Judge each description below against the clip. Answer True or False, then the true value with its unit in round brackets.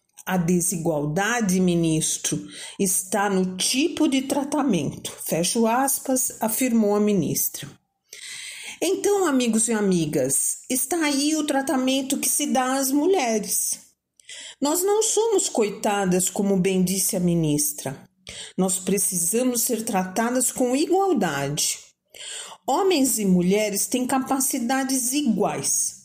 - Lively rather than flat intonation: True (6.9 semitones)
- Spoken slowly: True (110 wpm)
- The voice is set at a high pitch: True (230 Hz)